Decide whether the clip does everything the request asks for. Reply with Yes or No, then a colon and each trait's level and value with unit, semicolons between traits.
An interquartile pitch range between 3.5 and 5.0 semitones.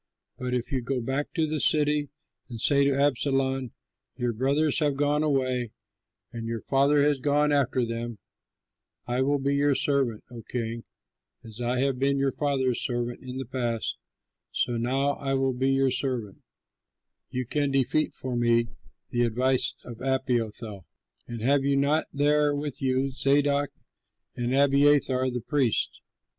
No: average, 2.7 semitones